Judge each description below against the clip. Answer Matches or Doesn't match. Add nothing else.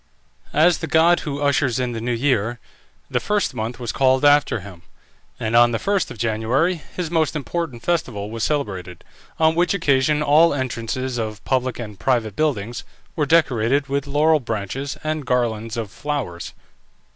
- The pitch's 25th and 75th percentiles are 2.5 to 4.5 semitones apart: Doesn't match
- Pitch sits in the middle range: Doesn't match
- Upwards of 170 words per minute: Doesn't match